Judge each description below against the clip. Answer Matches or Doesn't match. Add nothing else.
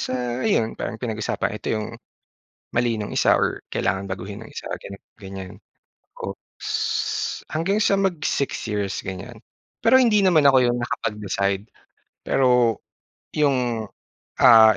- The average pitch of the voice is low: Matches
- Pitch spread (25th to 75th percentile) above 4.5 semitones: Matches